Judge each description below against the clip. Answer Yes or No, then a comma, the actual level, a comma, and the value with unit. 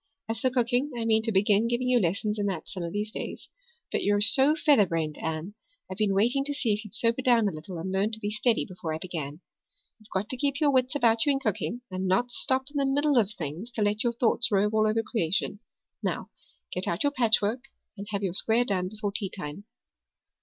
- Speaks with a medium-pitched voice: No, high, 215 Hz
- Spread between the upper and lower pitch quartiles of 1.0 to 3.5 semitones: No, average, 4.1 semitones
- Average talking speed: No, fast, 230 wpm